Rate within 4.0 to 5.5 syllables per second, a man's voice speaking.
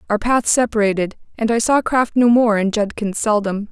No: 5.1 syllables/s; female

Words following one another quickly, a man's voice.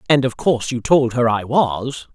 Yes: fast, 225 wpm; male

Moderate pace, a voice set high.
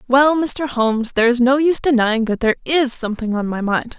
No: fast, 225 wpm; very high, 250 Hz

